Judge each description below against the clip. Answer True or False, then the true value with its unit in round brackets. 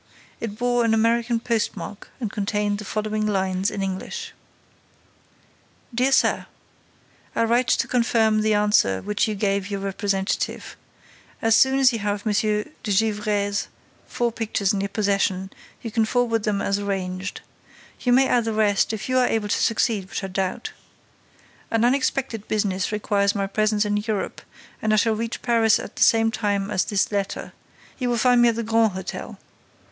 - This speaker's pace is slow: False (175 wpm)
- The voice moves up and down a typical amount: False (2.3 semitones)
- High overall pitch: True (215 Hz)